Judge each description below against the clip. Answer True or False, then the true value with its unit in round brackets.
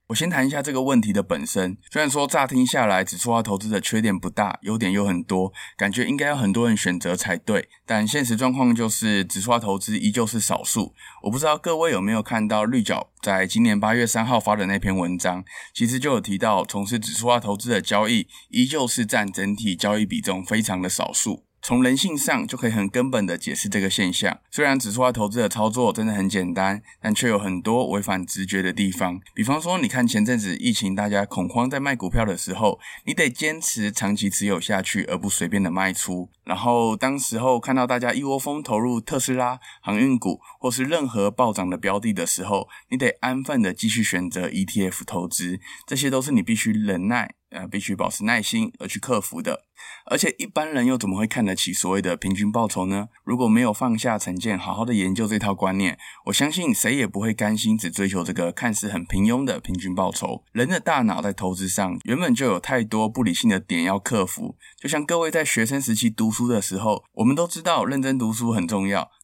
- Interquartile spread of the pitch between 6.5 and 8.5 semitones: False (5.5 semitones)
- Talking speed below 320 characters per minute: False (330 characters per minute)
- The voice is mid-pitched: False (110 Hz)